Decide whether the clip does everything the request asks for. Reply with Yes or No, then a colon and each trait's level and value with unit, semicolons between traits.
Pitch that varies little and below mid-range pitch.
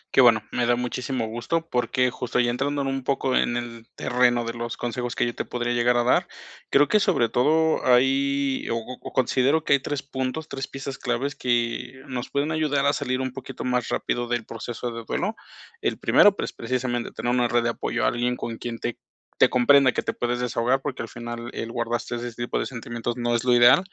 Yes: narrow, 2.1 semitones; low, 125 Hz